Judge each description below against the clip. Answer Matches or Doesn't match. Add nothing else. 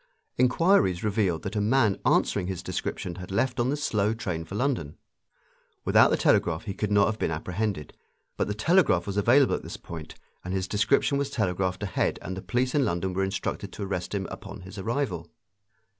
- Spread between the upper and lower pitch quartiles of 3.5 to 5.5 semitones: Matches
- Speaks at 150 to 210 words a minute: Matches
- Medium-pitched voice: Doesn't match